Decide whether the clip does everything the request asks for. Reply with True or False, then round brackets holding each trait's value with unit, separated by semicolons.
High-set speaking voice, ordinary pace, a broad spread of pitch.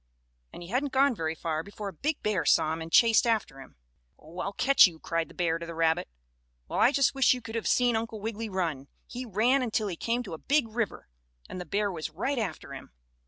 False (205 Hz; 240 wpm; 6.4 semitones)